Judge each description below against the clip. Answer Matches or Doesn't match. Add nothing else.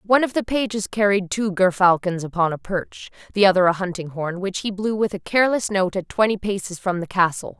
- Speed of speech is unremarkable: Doesn't match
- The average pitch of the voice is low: Doesn't match